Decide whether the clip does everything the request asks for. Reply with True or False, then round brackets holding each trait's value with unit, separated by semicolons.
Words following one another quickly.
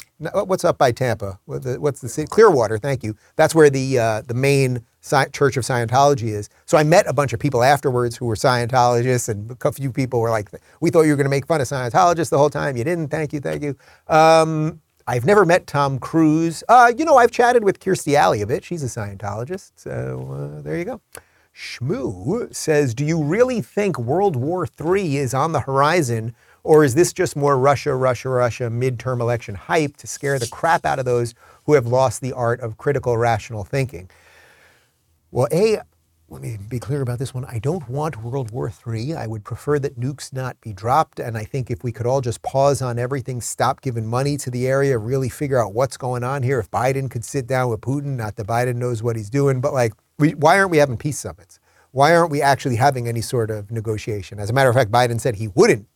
True (225 wpm)